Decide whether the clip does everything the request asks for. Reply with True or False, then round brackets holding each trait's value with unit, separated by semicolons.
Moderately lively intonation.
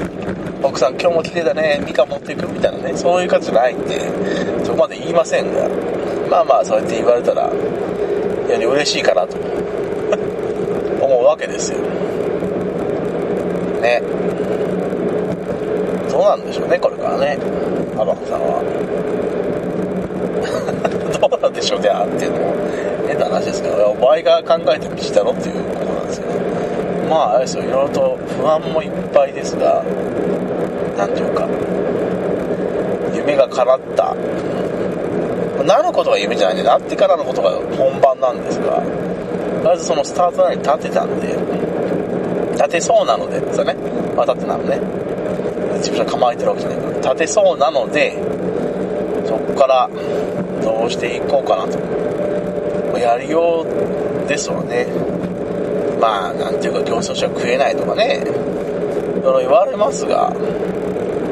True (4.8 semitones)